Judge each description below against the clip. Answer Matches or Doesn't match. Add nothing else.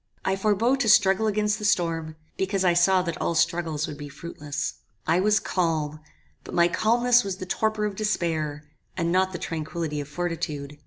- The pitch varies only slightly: Doesn't match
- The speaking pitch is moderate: Matches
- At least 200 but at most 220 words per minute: Doesn't match